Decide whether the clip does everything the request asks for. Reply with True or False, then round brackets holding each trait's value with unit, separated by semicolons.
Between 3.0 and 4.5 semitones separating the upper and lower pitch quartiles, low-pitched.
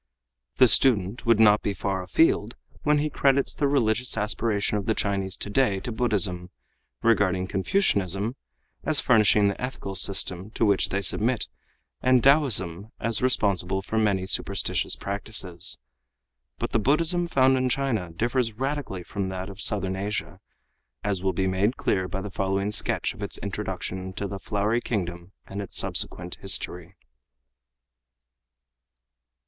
True (4.1 semitones; 105 Hz)